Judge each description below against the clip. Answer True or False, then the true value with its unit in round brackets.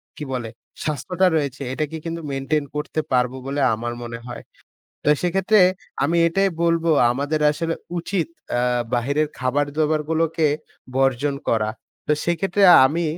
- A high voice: False (150 Hz)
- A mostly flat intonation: False (3.7 semitones)